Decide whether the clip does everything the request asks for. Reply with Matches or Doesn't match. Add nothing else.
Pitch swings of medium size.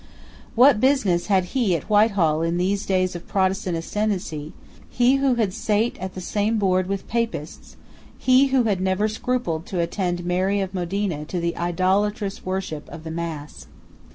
Matches